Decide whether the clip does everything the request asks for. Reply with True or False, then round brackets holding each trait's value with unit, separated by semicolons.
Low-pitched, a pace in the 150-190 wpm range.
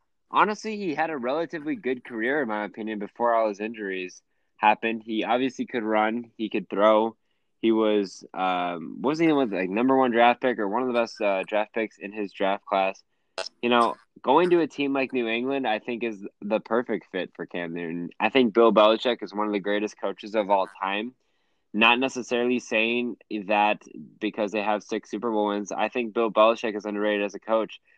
False (110 Hz; 205 wpm)